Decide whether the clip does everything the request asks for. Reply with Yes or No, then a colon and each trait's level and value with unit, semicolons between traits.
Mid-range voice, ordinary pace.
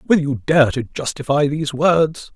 Yes: medium, 145 Hz; average, 180 wpm